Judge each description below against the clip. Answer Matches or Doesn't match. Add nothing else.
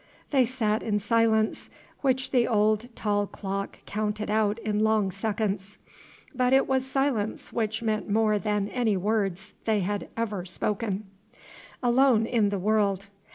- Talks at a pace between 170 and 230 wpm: Doesn't match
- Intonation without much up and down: Matches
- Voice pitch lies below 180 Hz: Doesn't match